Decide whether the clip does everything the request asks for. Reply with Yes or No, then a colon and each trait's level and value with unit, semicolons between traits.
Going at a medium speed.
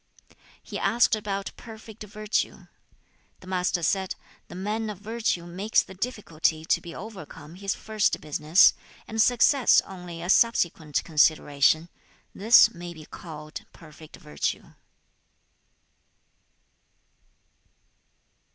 No: slow, 105 wpm